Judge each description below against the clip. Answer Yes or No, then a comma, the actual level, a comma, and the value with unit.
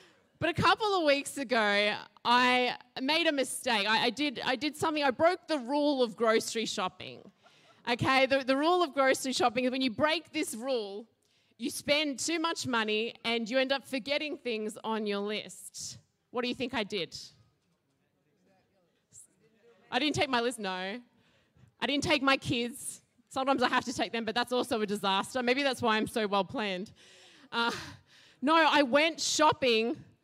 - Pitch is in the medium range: No, very high, 250 Hz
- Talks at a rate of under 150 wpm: No, average, 180 wpm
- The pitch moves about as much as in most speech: Yes, average, 4.4 semitones